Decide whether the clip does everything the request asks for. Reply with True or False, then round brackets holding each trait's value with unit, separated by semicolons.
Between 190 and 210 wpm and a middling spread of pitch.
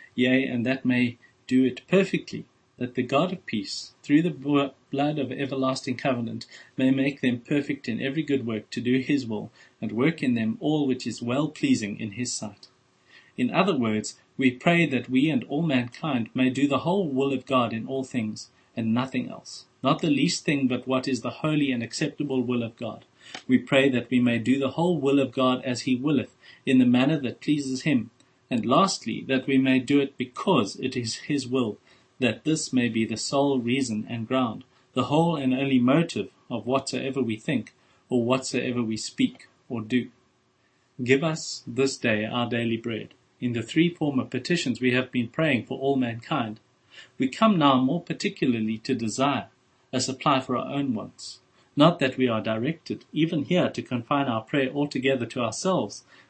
False (195 wpm; 2.3 semitones)